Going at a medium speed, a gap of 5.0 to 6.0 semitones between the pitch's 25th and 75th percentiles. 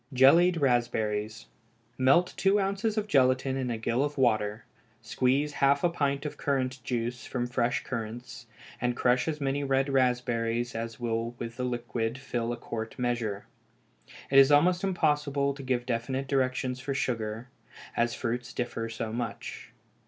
No: average, 155 wpm; average, 2.8 semitones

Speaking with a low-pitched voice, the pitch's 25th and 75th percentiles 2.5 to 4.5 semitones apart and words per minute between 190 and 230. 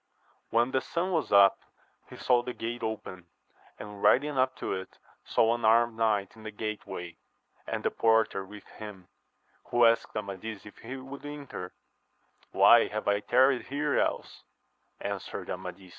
No: low, 115 Hz; average, 3.7 semitones; average, 165 wpm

